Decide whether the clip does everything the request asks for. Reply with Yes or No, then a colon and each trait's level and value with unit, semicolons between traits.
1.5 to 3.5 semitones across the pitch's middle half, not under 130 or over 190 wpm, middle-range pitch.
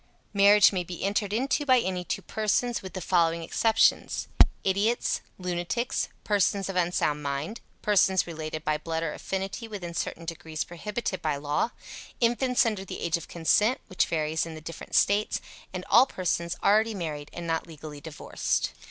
No: average, 4.3 semitones; average, 165 wpm; medium, 180 Hz